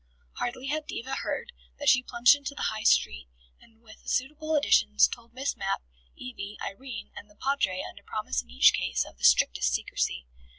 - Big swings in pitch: Yes, wide, 5.8 semitones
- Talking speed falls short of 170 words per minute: No, average, 180 wpm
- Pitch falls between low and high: No, high, 235 Hz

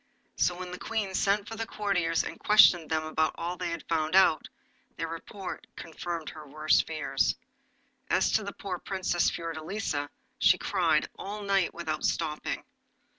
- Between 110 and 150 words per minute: No, average, 160 wpm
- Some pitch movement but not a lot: Yes, average, 3.8 semitones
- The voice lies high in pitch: No, medium, 175 Hz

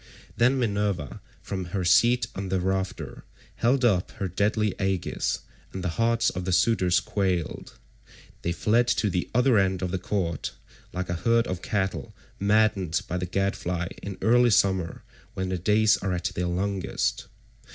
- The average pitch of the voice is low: Yes, very low, 95 Hz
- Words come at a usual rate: Yes, average, 160 wpm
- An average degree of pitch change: Yes, average, 3.1 semitones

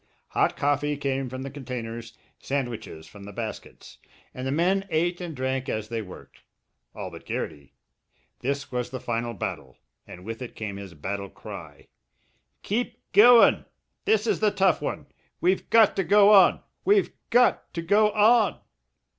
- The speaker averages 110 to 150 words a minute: No, average, 160 wpm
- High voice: No, medium, 140 Hz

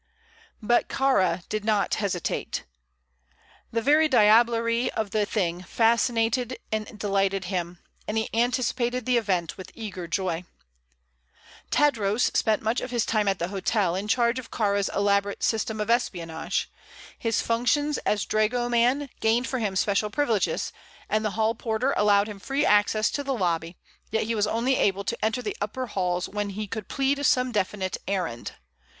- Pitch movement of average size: Yes, average, 3.2 semitones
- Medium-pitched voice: No, high, 215 Hz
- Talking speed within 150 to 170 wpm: Yes, average, 160 wpm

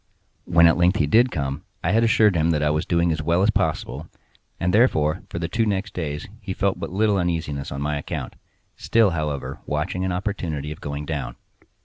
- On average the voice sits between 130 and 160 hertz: No, very low, 85 Hz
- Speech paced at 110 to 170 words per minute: No, fast, 205 wpm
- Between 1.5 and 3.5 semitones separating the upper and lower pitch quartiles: No, average, 4.1 semitones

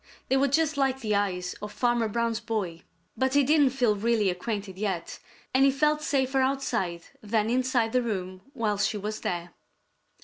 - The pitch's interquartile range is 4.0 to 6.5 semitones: Yes, average, 4.5 semitones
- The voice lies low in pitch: No, high, 230 Hz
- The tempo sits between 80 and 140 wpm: No, average, 175 wpm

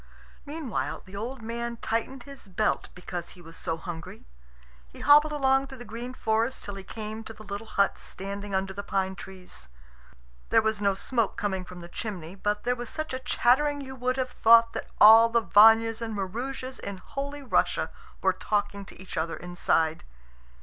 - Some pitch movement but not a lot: Yes, average, 4.5 semitones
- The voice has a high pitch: Yes, high, 220 Hz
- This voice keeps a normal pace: Yes, average, 185 wpm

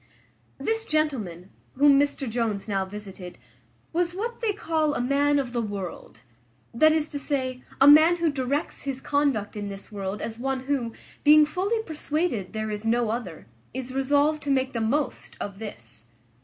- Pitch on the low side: No, very high, 265 Hz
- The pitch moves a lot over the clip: Yes, wide, 5.7 semitones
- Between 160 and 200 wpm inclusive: Yes, average, 170 wpm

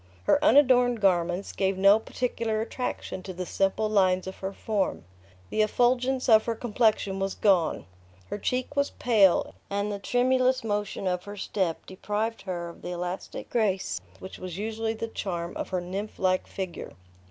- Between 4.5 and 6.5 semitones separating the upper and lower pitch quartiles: No, average, 3.4 semitones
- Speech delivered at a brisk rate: No, average, 165 wpm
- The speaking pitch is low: No, high, 205 Hz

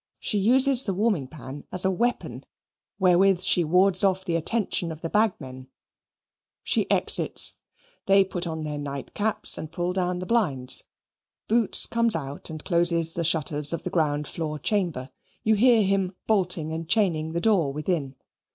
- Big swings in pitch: No, average, 4.3 semitones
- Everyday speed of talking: Yes, average, 165 wpm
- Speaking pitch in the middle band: Yes, medium, 175 Hz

